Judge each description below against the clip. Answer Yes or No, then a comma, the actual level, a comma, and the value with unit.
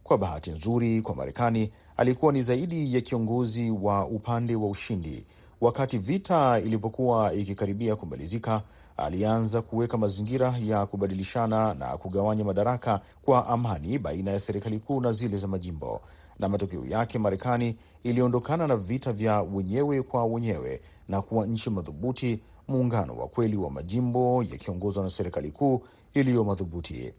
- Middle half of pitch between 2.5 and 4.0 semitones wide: Yes, average, 3.3 semitones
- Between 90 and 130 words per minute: No, fast, 140 wpm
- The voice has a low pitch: Yes, low, 110 Hz